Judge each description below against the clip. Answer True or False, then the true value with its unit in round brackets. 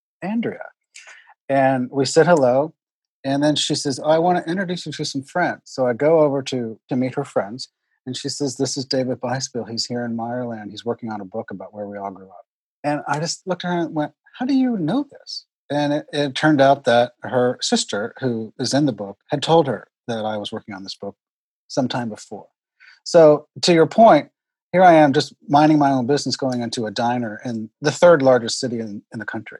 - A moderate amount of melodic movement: True (4.5 semitones)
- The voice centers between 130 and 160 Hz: True (135 Hz)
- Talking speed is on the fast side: True (225 wpm)